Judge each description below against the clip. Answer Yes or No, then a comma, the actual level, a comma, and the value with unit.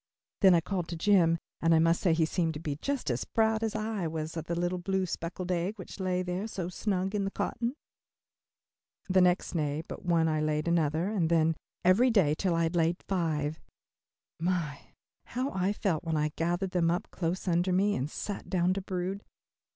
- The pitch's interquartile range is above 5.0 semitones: No, average, 2.8 semitones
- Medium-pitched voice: Yes, medium, 175 Hz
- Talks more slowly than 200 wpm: No, fast, 205 wpm